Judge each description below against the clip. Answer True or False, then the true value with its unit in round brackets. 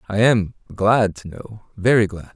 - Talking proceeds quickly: False (180 wpm)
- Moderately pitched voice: False (105 Hz)